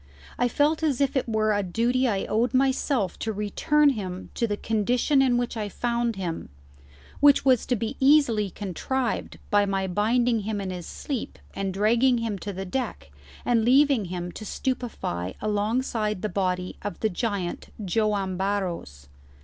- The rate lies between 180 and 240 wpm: No, average, 165 wpm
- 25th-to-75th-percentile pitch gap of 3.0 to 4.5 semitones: Yes, average, 4.2 semitones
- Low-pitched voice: No, high, 215 Hz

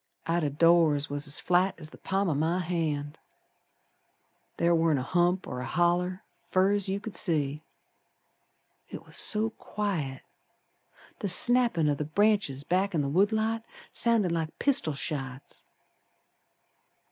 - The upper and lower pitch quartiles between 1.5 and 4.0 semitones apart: No, average, 4.8 semitones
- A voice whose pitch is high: No, medium, 170 Hz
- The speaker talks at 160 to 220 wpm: No, average, 145 wpm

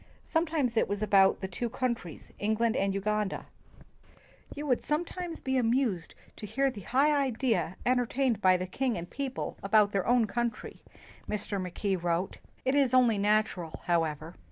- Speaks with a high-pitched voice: Yes, high, 220 Hz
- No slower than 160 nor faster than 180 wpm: Yes, average, 165 wpm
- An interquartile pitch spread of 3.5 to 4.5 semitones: No, average, 5.0 semitones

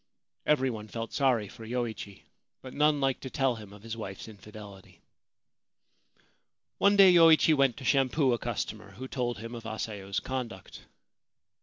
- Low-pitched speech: Yes, low, 120 Hz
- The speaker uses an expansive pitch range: No, average, 3.9 semitones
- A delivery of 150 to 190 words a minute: Yes, average, 155 wpm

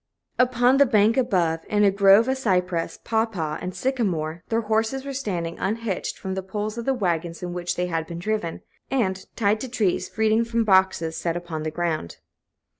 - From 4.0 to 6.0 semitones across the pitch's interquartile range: Yes, average, 4.7 semitones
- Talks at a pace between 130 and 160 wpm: No, average, 190 wpm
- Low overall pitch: No, high, 195 Hz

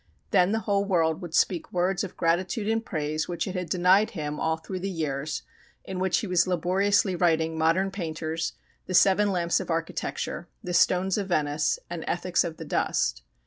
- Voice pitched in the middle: Yes, medium, 175 Hz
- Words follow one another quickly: No, average, 185 wpm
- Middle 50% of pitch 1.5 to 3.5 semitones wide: Yes, average, 2.8 semitones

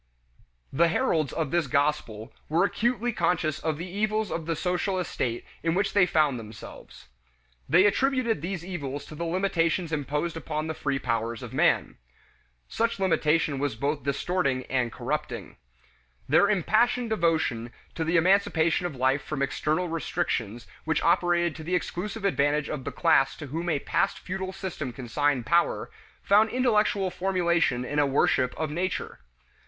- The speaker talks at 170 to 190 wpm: No, average, 155 wpm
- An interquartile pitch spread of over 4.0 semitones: Yes, average, 4.7 semitones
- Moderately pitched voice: Yes, medium, 165 Hz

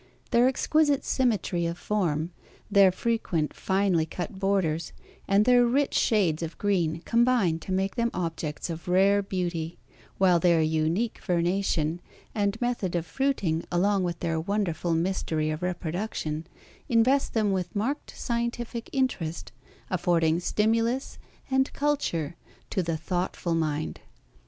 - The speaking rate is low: Yes, slow, 130 wpm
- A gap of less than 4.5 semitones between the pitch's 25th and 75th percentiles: No, average, 5.2 semitones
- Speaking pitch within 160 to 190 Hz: Yes, medium, 185 Hz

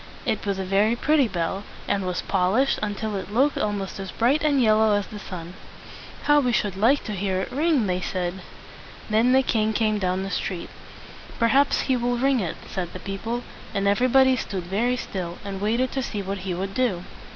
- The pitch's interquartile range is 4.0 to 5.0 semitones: Yes, average, 4.4 semitones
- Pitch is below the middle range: No, high, 210 Hz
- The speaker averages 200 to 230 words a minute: Yes, fast, 205 wpm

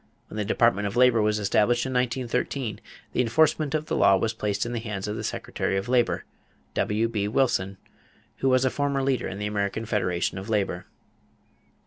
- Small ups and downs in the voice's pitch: No, average, 3.6 semitones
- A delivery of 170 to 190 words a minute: Yes, average, 185 wpm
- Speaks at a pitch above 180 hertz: No, low, 115 Hz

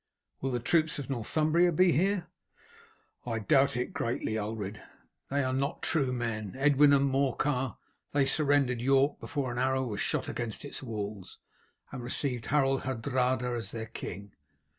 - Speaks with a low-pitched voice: Yes, low, 130 Hz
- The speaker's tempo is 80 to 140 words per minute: No, average, 155 wpm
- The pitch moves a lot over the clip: No, average, 3.3 semitones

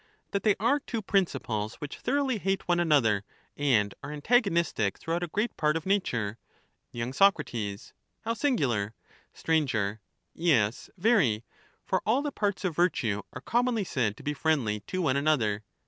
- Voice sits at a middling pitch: Yes, medium, 160 Hz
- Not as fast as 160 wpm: No, average, 165 wpm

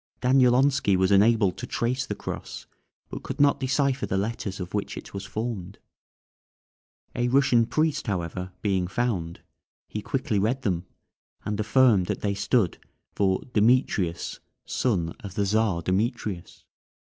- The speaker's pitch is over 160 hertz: No, low, 105 Hz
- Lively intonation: No, average, 4.8 semitones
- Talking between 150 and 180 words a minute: No, average, 140 wpm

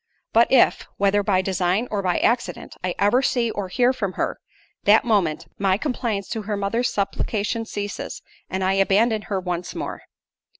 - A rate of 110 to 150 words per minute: No, average, 170 wpm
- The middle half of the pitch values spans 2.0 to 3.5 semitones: Yes, average, 3.1 semitones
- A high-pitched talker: Yes, high, 205 Hz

